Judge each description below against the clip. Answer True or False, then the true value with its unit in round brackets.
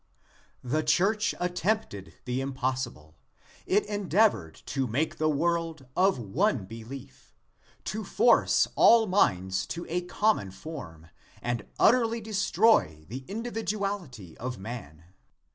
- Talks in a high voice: False (155 Hz)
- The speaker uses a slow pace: True (110 wpm)